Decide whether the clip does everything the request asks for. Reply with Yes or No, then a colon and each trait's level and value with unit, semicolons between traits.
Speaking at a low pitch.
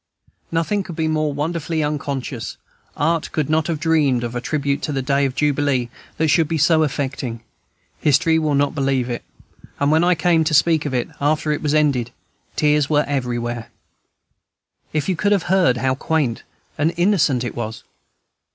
No: medium, 150 Hz